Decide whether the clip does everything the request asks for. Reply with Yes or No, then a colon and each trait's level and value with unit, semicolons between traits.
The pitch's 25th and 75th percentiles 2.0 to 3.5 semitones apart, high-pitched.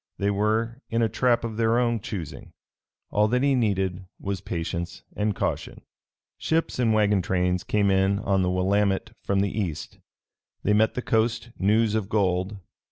No: average, 2.8 semitones; low, 105 Hz